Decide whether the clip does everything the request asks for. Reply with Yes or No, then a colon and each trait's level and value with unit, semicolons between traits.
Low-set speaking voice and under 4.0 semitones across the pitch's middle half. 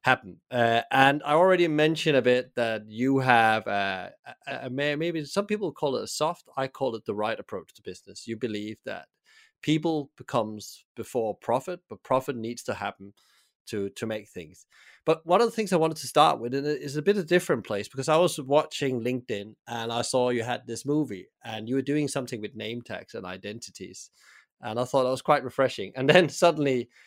No: low, 130 Hz; average, 4.8 semitones